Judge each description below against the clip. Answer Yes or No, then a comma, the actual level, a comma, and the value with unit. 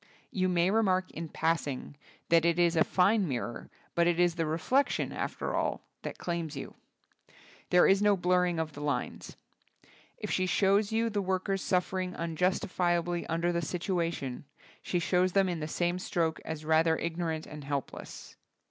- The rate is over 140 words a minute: Yes, average, 170 wpm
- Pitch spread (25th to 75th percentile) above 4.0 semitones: No, narrow, 2.4 semitones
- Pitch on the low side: No, medium, 175 Hz